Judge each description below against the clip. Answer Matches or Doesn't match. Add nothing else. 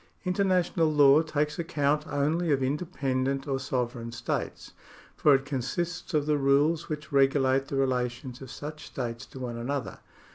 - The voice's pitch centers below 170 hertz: Matches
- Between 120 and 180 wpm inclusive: Matches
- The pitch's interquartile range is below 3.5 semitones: Matches